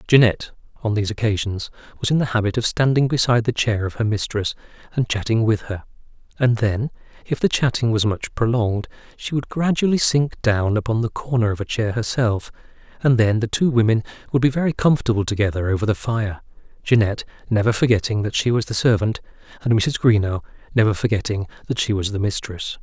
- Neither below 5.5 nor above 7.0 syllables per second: Yes, 6.0 syllables/s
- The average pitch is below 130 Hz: Yes, low, 115 Hz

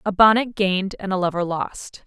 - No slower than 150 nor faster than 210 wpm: Yes, fast, 205 wpm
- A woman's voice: Yes, female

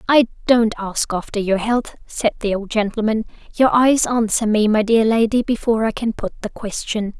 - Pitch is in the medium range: No, high, 220 Hz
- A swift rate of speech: No, average, 190 wpm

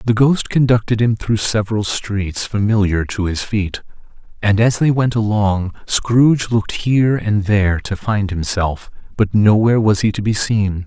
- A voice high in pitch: No, low, 105 Hz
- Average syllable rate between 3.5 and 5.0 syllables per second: Yes, 4.6 syllables/s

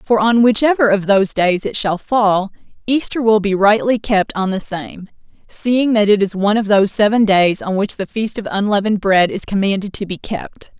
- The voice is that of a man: No, female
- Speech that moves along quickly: Yes, fast, 210 wpm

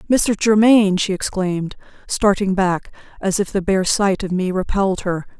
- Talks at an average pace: Yes, average, 165 wpm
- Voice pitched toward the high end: Yes, high, 195 Hz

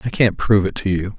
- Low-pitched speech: Yes, low, 100 Hz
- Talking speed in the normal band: No, fast, 305 wpm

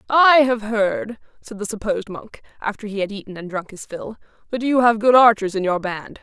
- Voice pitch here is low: No, high, 215 Hz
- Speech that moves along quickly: Yes, fast, 220 wpm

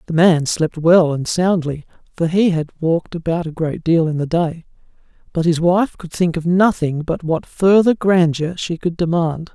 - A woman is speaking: No, male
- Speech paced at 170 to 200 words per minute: Yes, average, 195 wpm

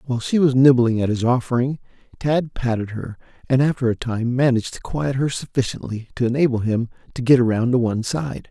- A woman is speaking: No, male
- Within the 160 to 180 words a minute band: No, average, 200 wpm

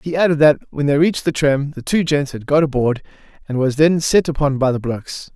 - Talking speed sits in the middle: No, fast, 245 wpm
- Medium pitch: Yes, medium, 145 Hz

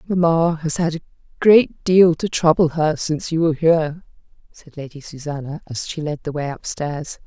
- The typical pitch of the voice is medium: Yes, medium, 160 Hz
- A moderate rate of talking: Yes, average, 180 wpm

